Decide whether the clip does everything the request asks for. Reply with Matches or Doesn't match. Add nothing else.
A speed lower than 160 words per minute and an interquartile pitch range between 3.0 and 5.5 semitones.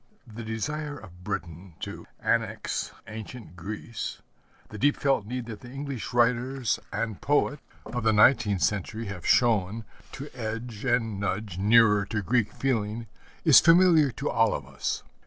Matches